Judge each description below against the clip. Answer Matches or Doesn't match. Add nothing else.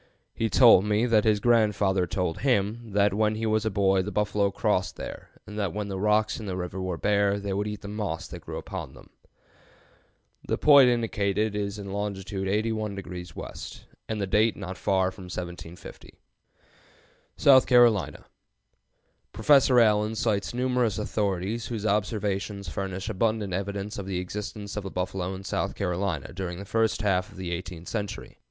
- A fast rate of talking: Doesn't match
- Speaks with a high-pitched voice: Doesn't match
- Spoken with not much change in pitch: Matches